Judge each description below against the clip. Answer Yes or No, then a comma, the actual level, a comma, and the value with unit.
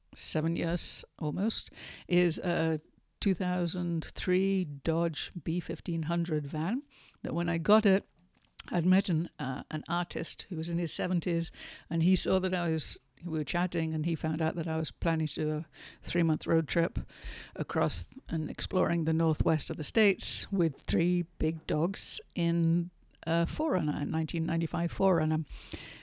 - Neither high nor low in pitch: Yes, medium, 165 Hz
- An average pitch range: No, narrow, 1.7 semitones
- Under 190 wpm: Yes, average, 155 wpm